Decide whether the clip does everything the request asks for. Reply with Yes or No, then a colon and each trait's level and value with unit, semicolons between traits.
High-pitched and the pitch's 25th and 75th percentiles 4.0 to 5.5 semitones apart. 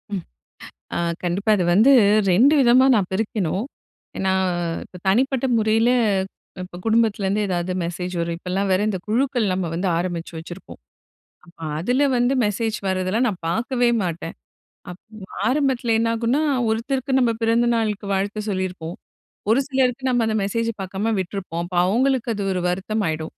Yes: high, 210 Hz; average, 4.6 semitones